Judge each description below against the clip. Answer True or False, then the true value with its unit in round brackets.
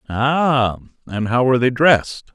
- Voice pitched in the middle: False (125 Hz)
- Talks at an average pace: True (155 wpm)